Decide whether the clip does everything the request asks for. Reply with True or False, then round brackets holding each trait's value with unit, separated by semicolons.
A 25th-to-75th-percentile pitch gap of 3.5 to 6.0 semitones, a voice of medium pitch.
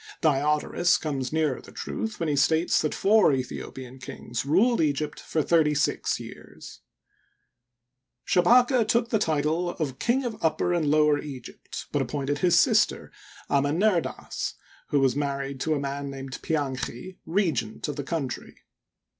True (4.1 semitones; 150 Hz)